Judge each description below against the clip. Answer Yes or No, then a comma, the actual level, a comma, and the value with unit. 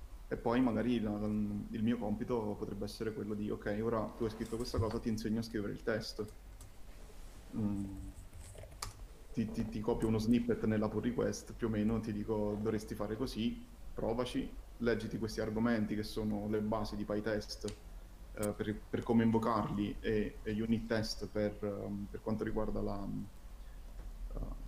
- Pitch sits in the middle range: No, low, 110 Hz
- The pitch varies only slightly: Yes, narrow, 1.3 semitones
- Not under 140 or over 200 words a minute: Yes, fast, 170 wpm